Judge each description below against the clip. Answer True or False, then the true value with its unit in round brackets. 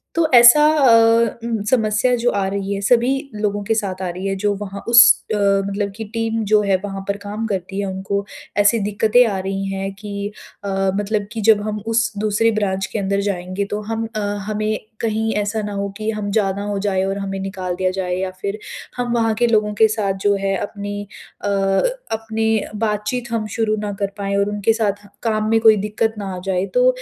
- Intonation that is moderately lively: False (2.1 semitones)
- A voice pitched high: True (205 Hz)